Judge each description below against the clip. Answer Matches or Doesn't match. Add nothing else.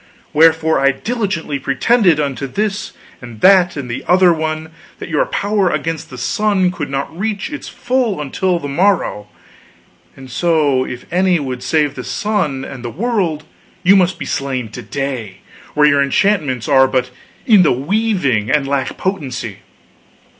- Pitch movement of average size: Doesn't match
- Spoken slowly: Doesn't match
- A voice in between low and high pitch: Matches